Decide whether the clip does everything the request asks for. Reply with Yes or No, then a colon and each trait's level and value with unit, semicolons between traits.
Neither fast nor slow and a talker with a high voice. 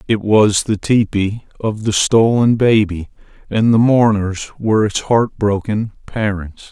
No: average, 145 wpm; low, 105 Hz